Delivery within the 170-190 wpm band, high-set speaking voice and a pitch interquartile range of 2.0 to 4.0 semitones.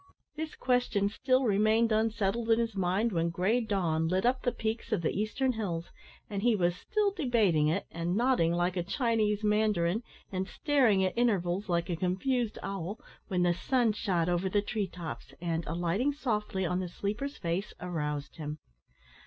No: average, 175 wpm; high, 200 Hz; average, 4.8 semitones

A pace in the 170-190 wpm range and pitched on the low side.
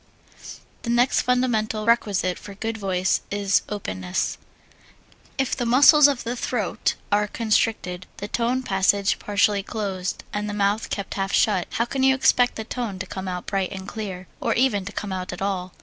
No: average, 180 wpm; high, 205 Hz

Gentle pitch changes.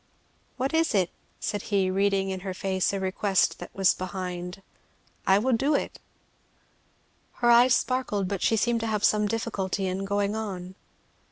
No: average, 3.2 semitones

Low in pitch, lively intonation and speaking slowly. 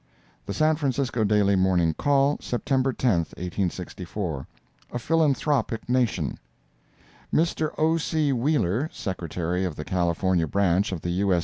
Yes: low, 105 Hz; wide, 7.5 semitones; slow, 125 wpm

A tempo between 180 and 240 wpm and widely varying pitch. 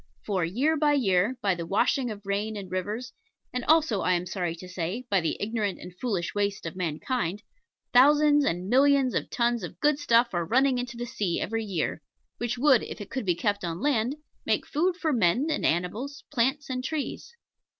Yes: average, 200 wpm; wide, 6.2 semitones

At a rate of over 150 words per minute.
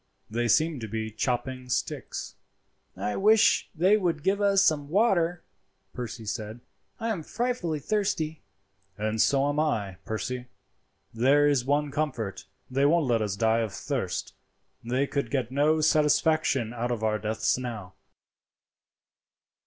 No: average, 140 wpm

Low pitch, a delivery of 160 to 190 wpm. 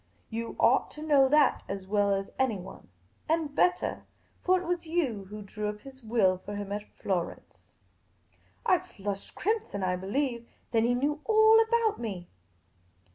No: high, 235 Hz; average, 165 wpm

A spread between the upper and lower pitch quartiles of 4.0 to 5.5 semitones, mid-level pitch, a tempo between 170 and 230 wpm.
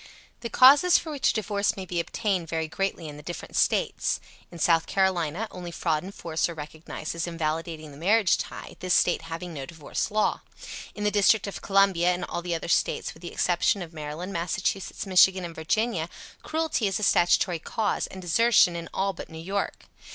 No: average, 3.4 semitones; medium, 175 Hz; average, 195 wpm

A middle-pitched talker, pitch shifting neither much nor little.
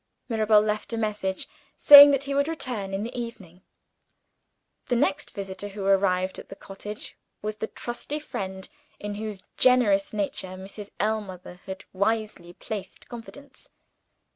No: high, 210 Hz; average, 3.1 semitones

